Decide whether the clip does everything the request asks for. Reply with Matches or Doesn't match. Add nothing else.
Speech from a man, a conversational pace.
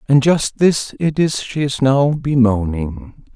Matches